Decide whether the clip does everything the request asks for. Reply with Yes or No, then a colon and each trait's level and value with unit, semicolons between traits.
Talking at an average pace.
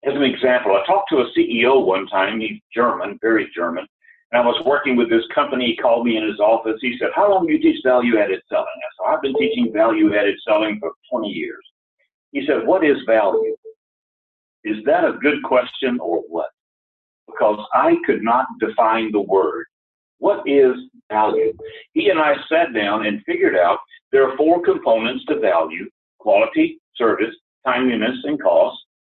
Yes: average, 180 wpm